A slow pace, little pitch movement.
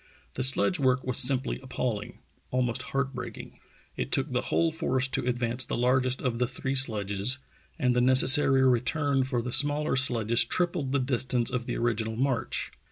No: average, 175 wpm; narrow, 1.7 semitones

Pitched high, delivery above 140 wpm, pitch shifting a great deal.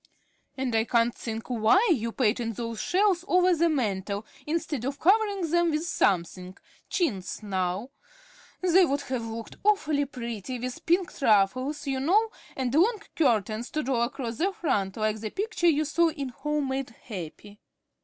Yes: very high, 260 Hz; average, 160 wpm; wide, 6.9 semitones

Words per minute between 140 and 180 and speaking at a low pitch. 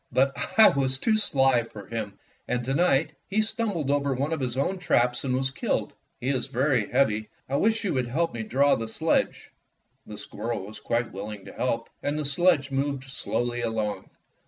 No: average, 195 wpm; low, 130 Hz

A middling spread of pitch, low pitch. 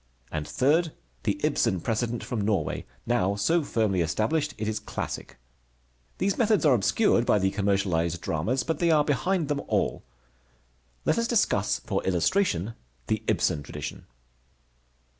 No: wide, 8.5 semitones; low, 115 Hz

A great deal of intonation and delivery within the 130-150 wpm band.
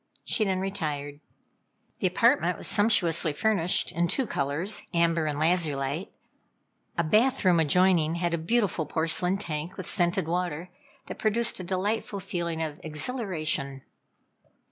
No: average, 3.6 semitones; slow, 135 wpm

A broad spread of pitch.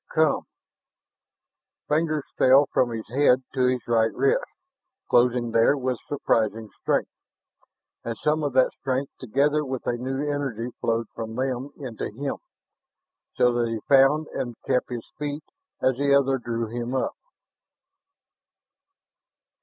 No: average, 3.2 semitones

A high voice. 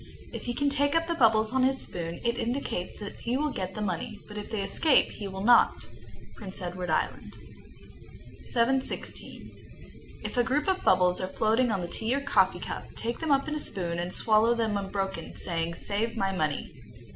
Yes: high, 220 Hz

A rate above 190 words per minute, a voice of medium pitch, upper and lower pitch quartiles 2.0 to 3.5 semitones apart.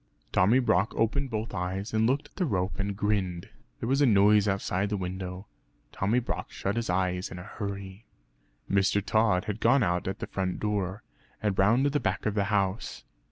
No: average, 200 wpm; low, 100 Hz; average, 2.8 semitones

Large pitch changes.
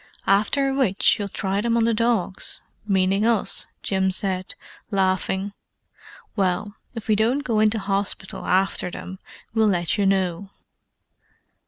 No: narrow, 2.6 semitones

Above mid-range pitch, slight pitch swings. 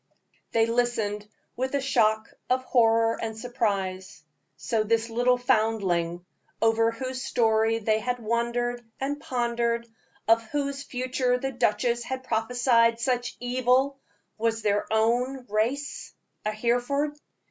Yes: high, 235 Hz; narrow, 2.2 semitones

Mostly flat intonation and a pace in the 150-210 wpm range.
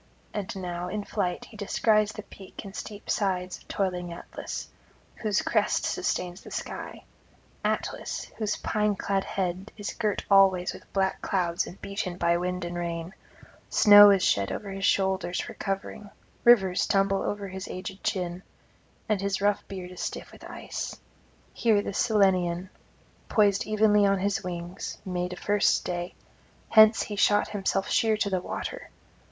Yes: narrow, 2.3 semitones; average, 160 wpm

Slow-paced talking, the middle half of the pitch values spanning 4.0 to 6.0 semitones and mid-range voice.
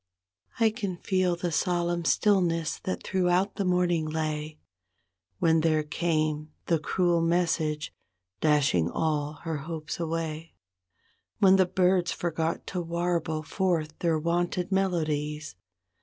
No: slow, 120 wpm; narrow, 2.5 semitones; medium, 165 Hz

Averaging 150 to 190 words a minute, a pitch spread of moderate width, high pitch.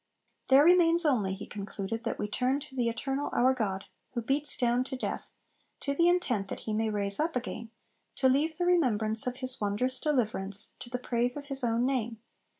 No: average, 200 wpm; average, 4.2 semitones; very high, 250 Hz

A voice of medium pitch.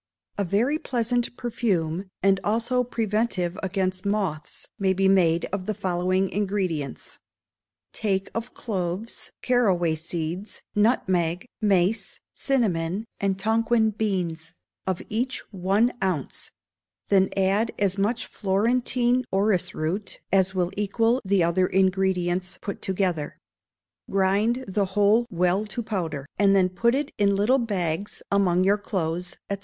No: high, 195 Hz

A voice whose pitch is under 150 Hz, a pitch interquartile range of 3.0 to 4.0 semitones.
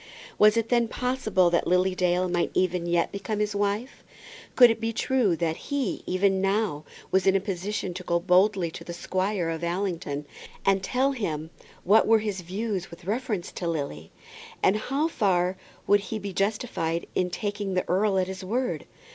No: high, 190 Hz; average, 3.3 semitones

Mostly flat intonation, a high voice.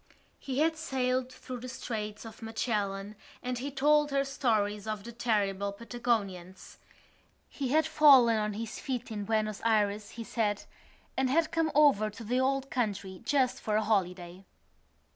No: average, 4.0 semitones; high, 230 Hz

